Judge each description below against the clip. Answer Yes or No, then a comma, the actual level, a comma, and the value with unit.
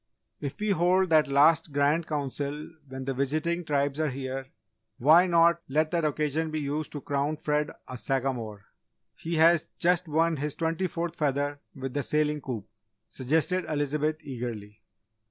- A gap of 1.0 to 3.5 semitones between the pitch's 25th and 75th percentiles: Yes, average, 2.9 semitones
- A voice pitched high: No, medium, 150 Hz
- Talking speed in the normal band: Yes, average, 155 wpm